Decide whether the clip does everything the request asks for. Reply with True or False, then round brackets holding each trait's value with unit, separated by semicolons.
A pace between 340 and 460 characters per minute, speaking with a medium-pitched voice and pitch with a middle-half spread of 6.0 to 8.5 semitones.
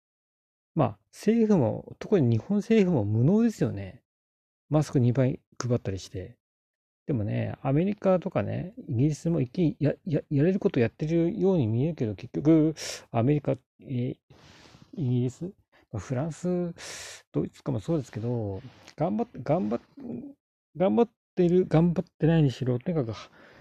False (290 characters per minute; 150 Hz; 6.8 semitones)